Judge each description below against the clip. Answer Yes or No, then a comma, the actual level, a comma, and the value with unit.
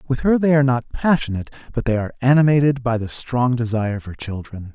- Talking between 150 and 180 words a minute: No, average, 200 wpm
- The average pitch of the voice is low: Yes, low, 125 Hz